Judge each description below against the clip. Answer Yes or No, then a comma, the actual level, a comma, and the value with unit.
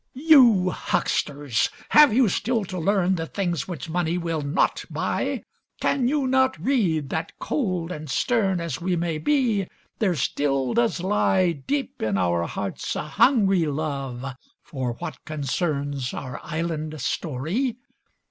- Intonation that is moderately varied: No, wide, 6.5 semitones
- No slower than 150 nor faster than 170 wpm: No, average, 140 wpm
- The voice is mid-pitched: Yes, medium, 170 Hz